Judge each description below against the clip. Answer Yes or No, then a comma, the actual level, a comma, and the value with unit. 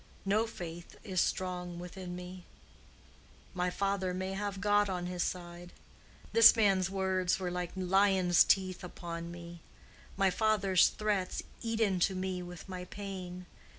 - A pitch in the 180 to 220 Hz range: Yes, medium, 185 Hz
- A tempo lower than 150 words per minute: Yes, average, 140 wpm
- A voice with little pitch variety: Yes, narrow, 1.7 semitones